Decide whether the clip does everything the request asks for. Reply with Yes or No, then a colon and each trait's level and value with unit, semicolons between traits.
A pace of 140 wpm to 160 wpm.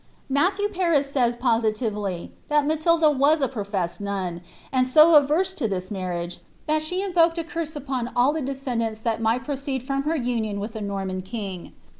No: average, 190 wpm